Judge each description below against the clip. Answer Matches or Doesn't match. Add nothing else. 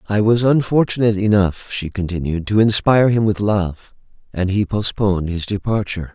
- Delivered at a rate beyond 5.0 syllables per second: Matches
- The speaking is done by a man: Matches